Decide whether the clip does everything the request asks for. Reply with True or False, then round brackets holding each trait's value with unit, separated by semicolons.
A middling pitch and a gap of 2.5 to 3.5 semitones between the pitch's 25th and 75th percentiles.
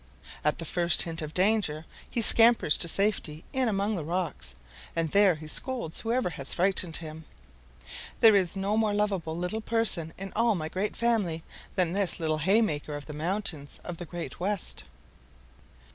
False (180 Hz; 4.7 semitones)